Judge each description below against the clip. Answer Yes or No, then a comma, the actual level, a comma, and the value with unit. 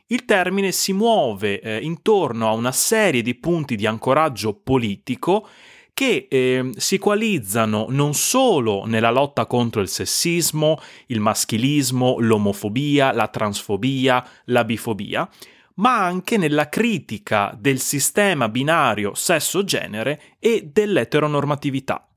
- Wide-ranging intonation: Yes, wide, 7.2 semitones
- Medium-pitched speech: No, low, 130 Hz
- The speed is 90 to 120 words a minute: Yes, slow, 115 wpm